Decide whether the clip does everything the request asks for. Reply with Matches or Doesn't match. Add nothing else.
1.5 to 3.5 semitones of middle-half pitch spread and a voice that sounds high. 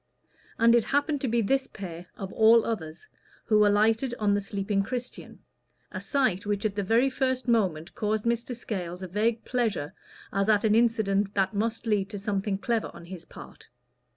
Matches